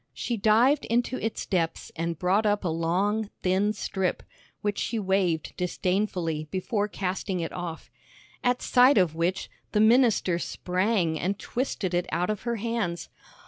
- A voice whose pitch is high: Yes, high, 195 Hz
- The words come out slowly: No, average, 150 wpm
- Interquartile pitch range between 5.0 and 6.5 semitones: No, average, 3.8 semitones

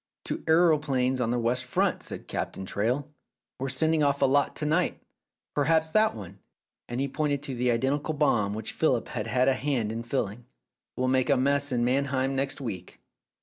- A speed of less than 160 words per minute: No, fast, 205 wpm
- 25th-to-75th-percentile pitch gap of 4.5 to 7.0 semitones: No, average, 3.1 semitones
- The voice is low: Yes, low, 130 Hz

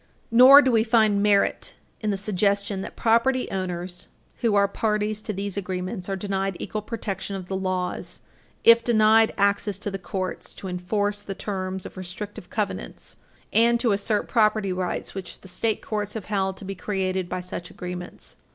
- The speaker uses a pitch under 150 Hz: No, high, 200 Hz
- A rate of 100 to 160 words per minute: No, average, 175 wpm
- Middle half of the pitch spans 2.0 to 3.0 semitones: Yes, narrow, 2.4 semitones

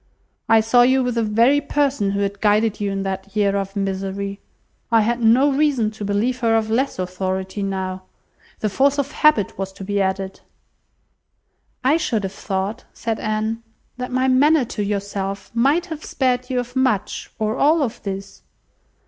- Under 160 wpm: No, average, 175 wpm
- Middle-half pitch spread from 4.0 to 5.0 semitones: Yes, average, 4.5 semitones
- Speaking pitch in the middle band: No, high, 215 Hz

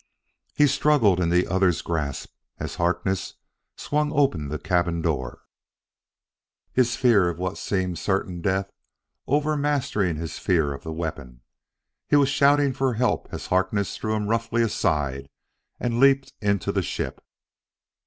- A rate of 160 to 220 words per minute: No, average, 145 wpm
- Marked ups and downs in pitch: Yes, wide, 7.1 semitones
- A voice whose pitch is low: Yes, very low, 95 Hz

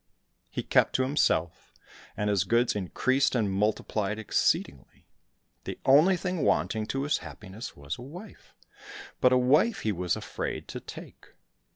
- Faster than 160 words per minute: No, average, 150 wpm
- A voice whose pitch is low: Yes, low, 115 Hz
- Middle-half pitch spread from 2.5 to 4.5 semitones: No, wide, 5.4 semitones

